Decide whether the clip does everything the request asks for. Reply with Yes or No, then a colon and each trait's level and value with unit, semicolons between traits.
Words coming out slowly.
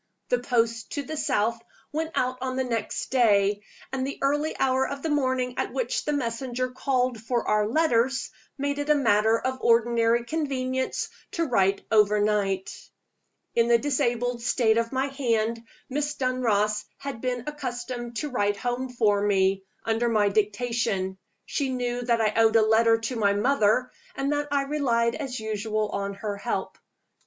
No: average, 165 wpm